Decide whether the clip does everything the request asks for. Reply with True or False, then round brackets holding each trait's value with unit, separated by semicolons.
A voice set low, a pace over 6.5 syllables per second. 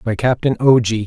False (120 Hz; 5.4 syllables/s)